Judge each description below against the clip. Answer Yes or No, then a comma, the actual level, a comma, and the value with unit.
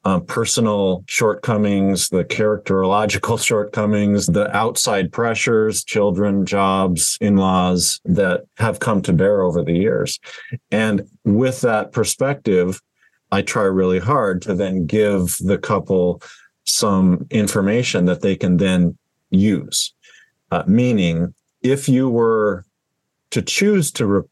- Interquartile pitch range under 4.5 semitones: Yes, average, 2.9 semitones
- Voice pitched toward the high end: No, low, 100 Hz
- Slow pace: Yes, slow, 120 wpm